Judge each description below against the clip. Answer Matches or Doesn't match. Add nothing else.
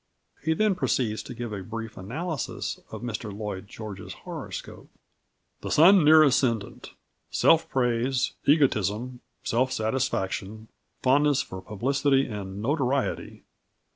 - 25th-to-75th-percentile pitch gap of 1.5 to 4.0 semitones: Doesn't match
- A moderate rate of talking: Doesn't match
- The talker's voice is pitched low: Matches